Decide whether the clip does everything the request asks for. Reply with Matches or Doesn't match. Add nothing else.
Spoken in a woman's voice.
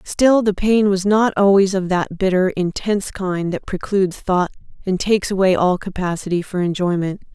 Matches